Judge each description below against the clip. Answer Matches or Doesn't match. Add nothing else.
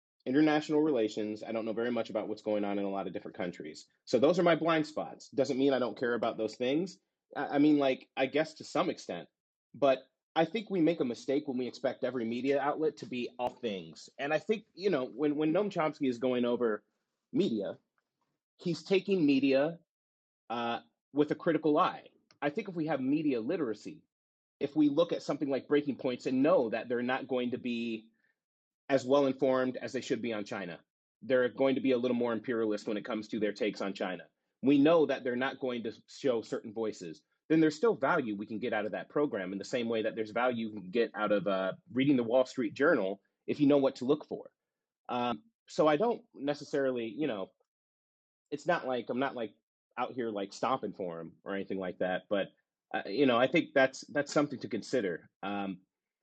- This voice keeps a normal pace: Doesn't match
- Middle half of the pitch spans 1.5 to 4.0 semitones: Doesn't match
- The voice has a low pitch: Matches